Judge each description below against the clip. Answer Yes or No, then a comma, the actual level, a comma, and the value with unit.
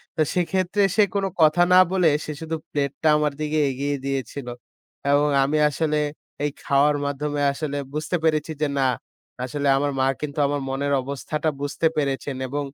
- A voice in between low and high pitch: Yes, medium, 145 Hz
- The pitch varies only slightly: Yes, narrow, 1.8 semitones